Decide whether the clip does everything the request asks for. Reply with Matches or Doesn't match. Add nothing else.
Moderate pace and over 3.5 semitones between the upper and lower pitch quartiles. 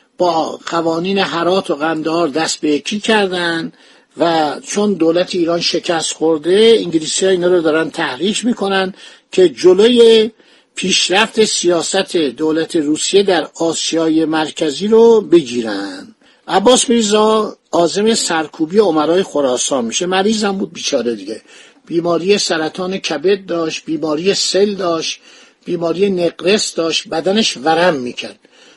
Matches